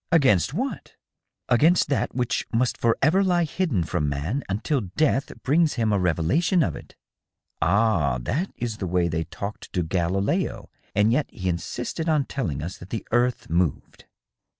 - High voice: No, low, 110 Hz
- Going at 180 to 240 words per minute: No, average, 170 wpm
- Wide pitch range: Yes, wide, 8.3 semitones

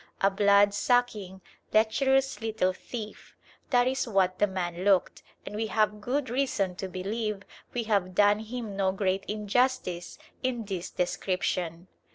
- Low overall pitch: No, high, 205 Hz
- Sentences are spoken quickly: No, average, 145 wpm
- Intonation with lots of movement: No, average, 3.4 semitones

